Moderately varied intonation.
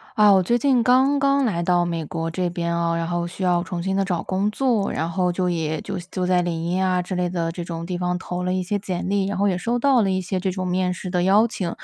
No: narrow, 2.2 semitones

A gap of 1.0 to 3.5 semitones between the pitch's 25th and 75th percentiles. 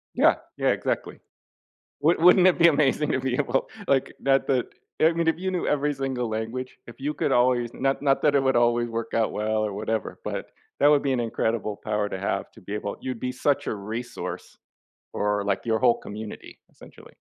No: average, 4.2 semitones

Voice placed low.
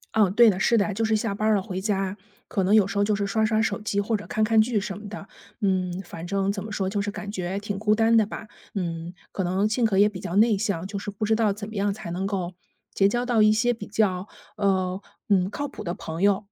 No: high, 205 Hz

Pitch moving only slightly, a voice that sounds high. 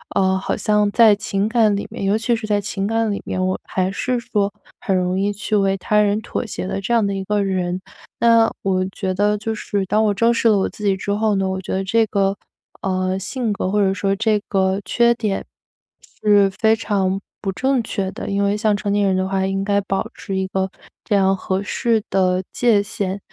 Yes: narrow, 1.9 semitones; high, 200 Hz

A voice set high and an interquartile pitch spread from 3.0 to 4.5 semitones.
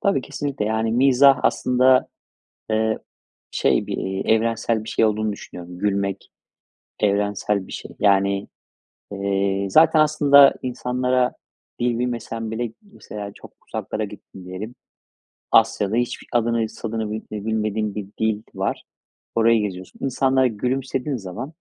No: low, 110 Hz; average, 3.5 semitones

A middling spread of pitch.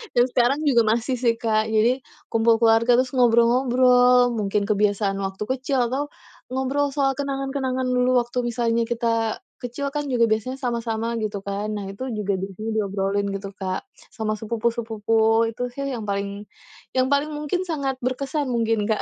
Yes: average, 3.0 semitones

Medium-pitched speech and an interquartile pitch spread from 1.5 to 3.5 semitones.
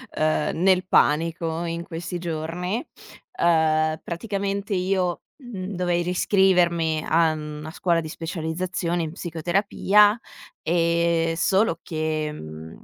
Yes: medium, 170 Hz; narrow, 2.4 semitones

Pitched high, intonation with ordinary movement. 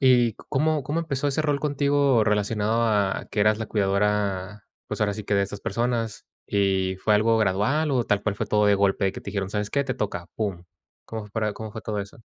No: low, 105 Hz; average, 3.1 semitones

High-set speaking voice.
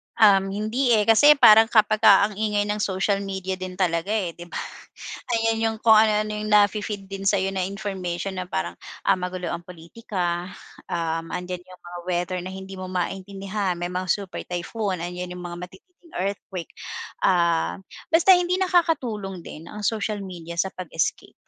Yes: high, 195 Hz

